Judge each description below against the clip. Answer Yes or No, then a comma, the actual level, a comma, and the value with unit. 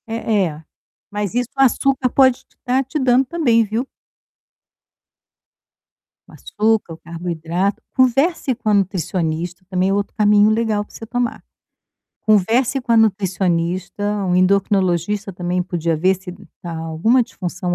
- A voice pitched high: Yes, high, 205 Hz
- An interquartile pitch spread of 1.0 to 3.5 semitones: No, average, 4.6 semitones